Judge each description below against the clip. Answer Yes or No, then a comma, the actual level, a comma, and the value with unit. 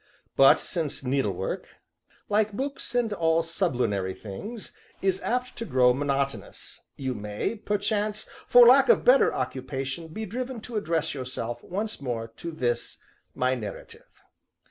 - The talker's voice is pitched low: No, medium, 160 Hz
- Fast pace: No, slow, 135 wpm